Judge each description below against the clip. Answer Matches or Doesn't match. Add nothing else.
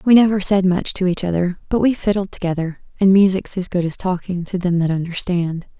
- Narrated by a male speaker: Doesn't match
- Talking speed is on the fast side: Matches